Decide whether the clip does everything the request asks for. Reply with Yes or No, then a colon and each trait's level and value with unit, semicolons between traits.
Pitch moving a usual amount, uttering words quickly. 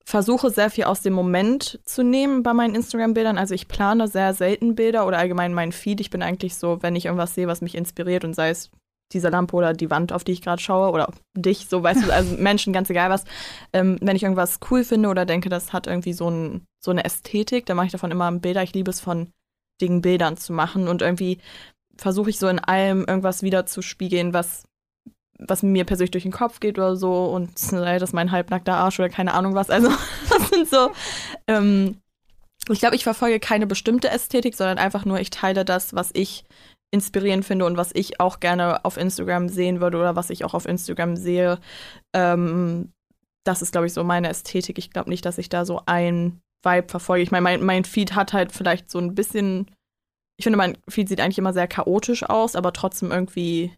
No: narrow, 2.1 semitones; fast, 220 wpm